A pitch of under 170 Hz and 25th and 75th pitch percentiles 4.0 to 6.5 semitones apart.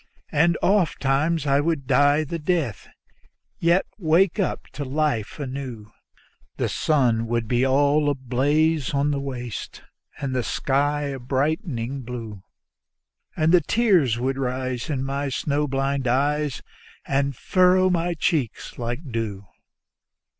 No: medium, 140 Hz; average, 3.4 semitones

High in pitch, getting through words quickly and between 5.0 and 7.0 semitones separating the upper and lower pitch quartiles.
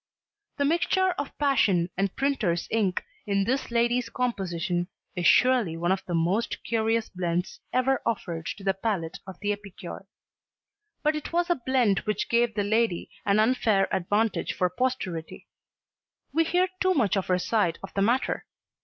No: high, 210 Hz; average, 160 wpm; wide, 5.5 semitones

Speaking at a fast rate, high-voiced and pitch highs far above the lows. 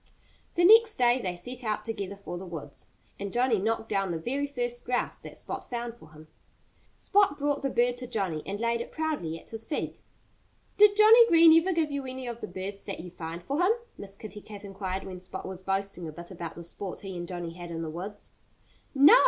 Yes: fast, 225 wpm; high, 210 Hz; wide, 6.4 semitones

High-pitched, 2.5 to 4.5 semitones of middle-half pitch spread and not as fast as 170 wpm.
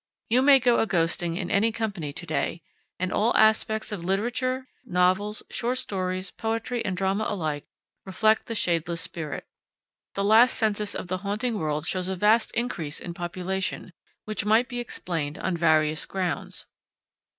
Yes: high, 195 Hz; average, 4.2 semitones; average, 160 wpm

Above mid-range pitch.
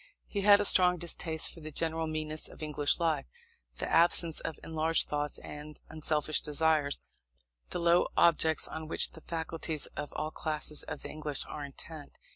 No: medium, 160 Hz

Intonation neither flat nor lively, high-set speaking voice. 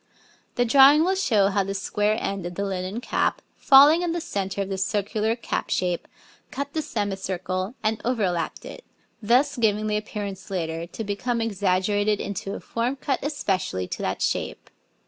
Yes: average, 4.2 semitones; high, 210 Hz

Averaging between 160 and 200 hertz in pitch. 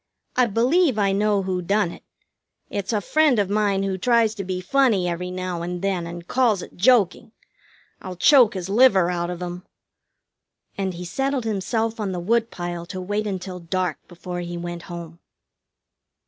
Yes: high, 190 Hz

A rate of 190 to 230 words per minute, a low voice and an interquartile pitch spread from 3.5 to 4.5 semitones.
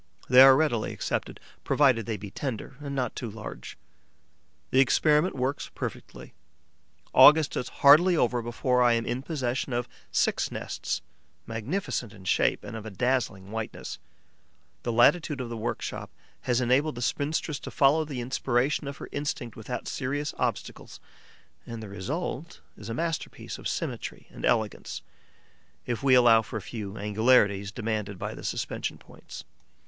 No: average, 155 wpm; low, 125 Hz; average, 3.9 semitones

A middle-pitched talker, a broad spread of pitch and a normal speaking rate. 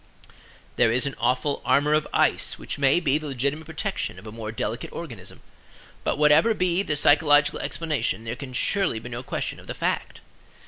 No: medium, 145 Hz; average, 4.2 semitones; average, 185 wpm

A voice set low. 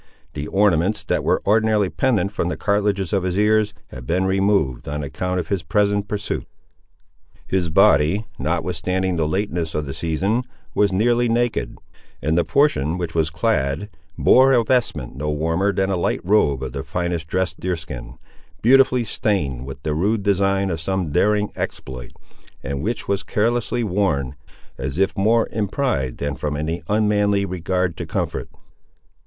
Yes: very low, 95 Hz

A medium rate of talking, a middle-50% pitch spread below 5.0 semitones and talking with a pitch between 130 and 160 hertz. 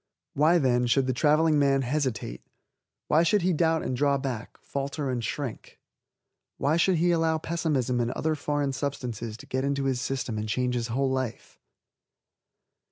Yes: average, 165 wpm; average, 3.6 semitones; low, 135 Hz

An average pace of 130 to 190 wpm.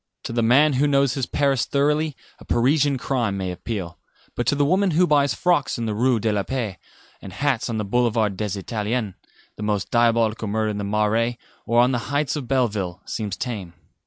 No: fast, 205 wpm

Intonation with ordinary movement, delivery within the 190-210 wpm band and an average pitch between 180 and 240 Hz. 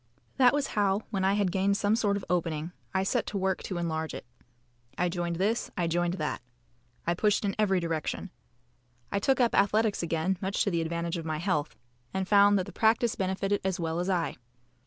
Yes: average, 3.1 semitones; fast, 205 wpm; high, 190 Hz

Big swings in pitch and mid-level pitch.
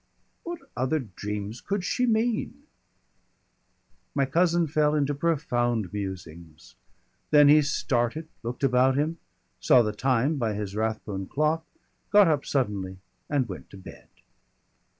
No: wide, 6.7 semitones; low, 130 Hz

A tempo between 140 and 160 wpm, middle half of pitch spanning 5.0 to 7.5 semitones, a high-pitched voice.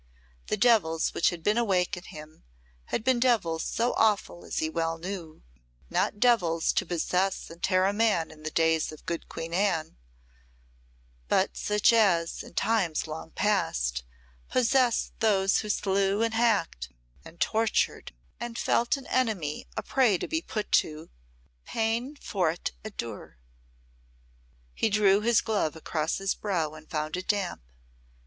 Yes: average, 155 wpm; wide, 5.5 semitones; high, 195 Hz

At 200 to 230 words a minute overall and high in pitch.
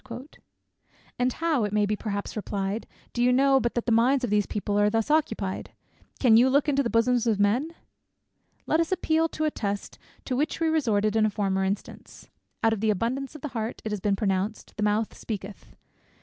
Yes: fast, 205 wpm; high, 225 Hz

